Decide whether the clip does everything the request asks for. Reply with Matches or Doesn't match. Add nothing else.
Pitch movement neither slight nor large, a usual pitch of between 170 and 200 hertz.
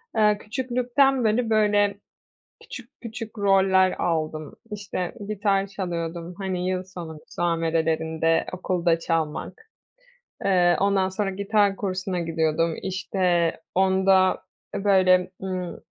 Matches